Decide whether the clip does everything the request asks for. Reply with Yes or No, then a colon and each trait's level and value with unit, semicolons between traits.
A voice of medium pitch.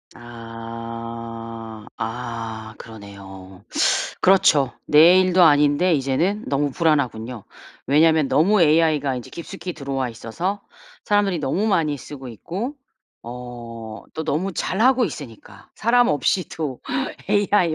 Yes: medium, 145 Hz